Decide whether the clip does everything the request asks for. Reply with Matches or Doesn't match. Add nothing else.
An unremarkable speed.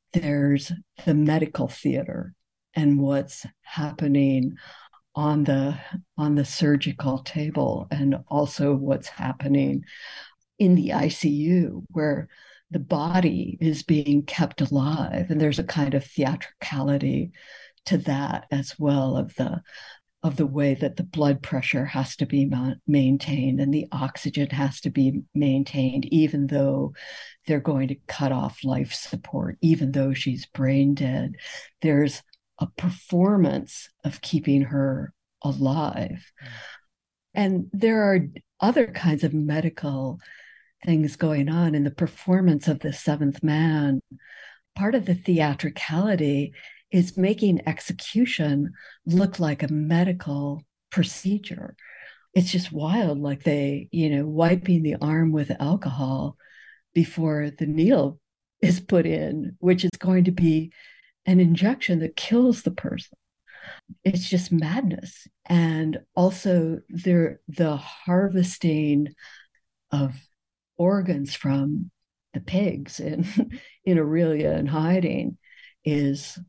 Doesn't match